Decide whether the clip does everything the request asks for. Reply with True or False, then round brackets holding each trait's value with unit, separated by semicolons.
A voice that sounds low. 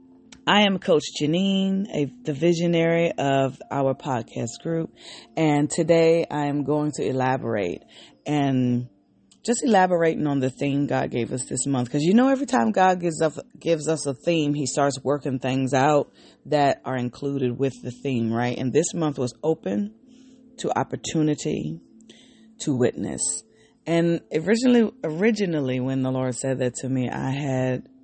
False (150 Hz)